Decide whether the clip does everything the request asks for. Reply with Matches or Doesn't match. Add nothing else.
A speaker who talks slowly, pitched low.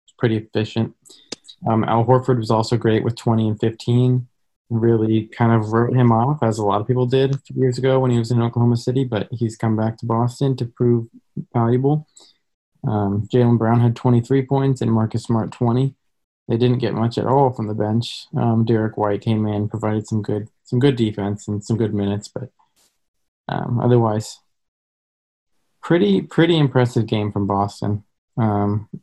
Doesn't match